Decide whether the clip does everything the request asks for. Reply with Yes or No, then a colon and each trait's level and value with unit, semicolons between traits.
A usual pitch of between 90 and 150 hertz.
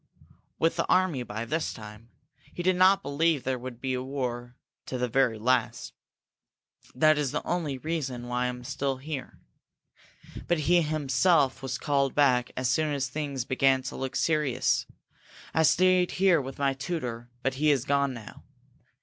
Yes: low, 135 Hz